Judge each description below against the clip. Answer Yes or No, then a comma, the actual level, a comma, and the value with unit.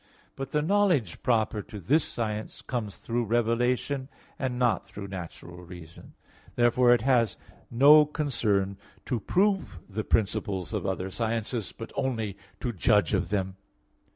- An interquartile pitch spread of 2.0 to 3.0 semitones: No, average, 4.4 semitones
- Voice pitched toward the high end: No, low, 115 Hz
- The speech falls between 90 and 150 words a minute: Yes, average, 140 wpm